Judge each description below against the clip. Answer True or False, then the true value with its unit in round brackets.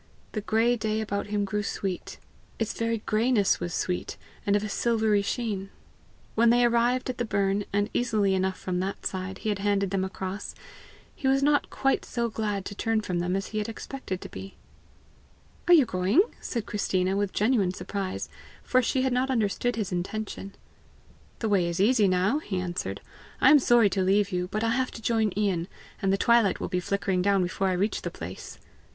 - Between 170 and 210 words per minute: True (200 wpm)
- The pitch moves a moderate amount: True (3.3 semitones)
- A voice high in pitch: True (205 Hz)